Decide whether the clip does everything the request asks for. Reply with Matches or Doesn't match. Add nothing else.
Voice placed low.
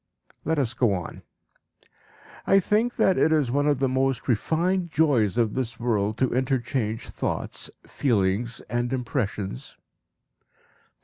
Matches